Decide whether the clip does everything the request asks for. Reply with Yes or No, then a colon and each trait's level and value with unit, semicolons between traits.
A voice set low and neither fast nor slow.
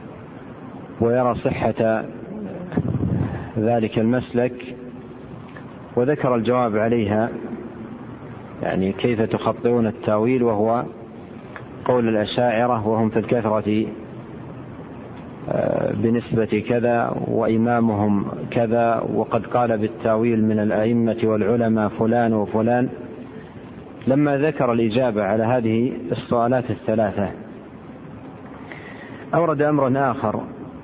Yes: low, 115 Hz; average, 75 wpm